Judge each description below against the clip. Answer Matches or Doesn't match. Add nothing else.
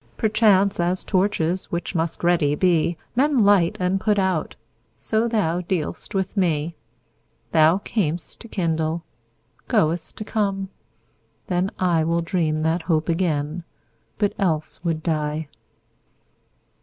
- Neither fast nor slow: Doesn't match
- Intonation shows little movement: Doesn't match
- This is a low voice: Doesn't match